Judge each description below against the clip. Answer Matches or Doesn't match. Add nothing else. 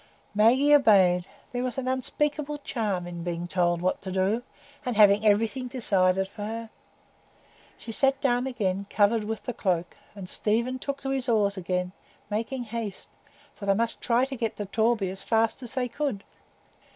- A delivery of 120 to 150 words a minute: Doesn't match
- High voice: Matches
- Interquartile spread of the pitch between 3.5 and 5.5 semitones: Matches